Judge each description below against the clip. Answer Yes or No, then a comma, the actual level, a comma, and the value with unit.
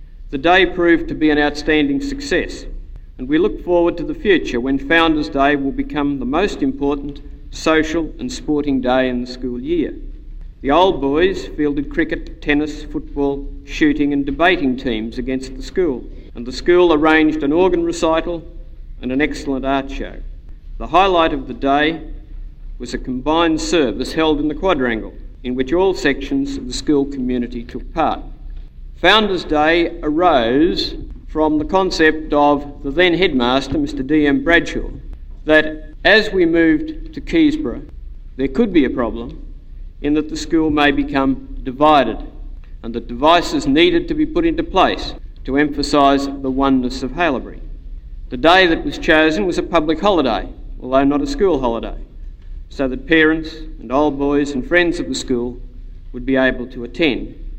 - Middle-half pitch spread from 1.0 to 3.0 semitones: No, average, 4.2 semitones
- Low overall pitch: No, medium, 145 Hz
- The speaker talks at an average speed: Yes, average, 165 wpm